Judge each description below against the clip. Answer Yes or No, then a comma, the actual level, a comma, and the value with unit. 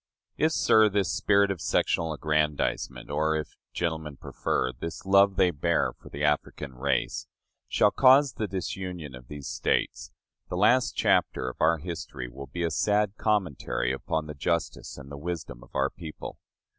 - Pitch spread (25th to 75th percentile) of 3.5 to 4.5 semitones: No, average, 5.2 semitones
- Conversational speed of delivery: Yes, average, 160 wpm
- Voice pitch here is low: Yes, very low, 80 Hz